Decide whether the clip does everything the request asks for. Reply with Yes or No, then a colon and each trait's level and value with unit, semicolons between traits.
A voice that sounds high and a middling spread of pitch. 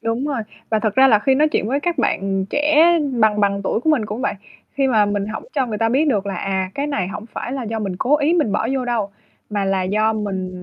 Yes: high, 220 Hz; average, 5.0 semitones